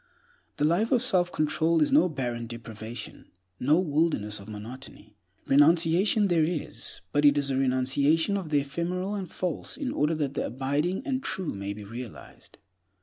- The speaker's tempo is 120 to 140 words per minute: No, average, 165 wpm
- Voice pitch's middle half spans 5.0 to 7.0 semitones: Yes, wide, 5.6 semitones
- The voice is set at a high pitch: No, medium, 150 Hz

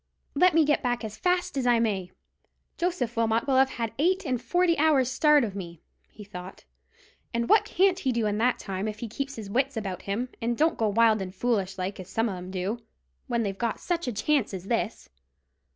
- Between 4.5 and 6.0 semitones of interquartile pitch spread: Yes, wide, 5.5 semitones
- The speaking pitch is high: Yes, high, 230 Hz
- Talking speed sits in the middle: No, fast, 220 wpm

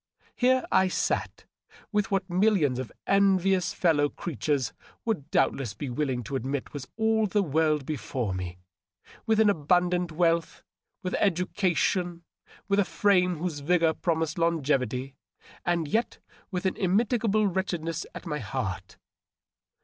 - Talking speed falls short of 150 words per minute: Yes, slow, 135 wpm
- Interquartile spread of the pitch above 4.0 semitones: Yes, average, 5.2 semitones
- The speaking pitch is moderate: Yes, medium, 170 Hz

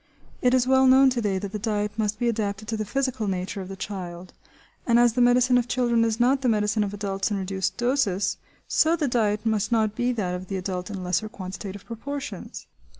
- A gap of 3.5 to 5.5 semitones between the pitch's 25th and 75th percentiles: Yes, average, 3.8 semitones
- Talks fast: Yes, fast, 220 wpm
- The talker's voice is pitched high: Yes, high, 215 Hz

